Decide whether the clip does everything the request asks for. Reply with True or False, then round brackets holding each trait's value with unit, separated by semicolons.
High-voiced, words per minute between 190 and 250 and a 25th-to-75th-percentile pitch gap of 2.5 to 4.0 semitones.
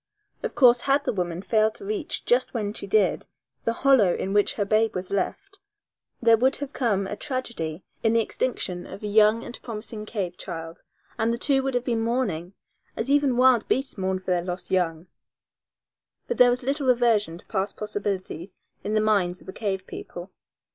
False (215 Hz; 195 wpm; 4.5 semitones)